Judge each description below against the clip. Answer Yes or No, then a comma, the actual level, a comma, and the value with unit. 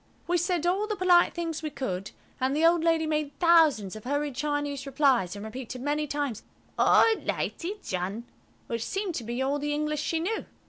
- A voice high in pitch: Yes, very high, 295 Hz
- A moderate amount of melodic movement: Yes, average, 4.6 semitones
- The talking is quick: No, average, 190 wpm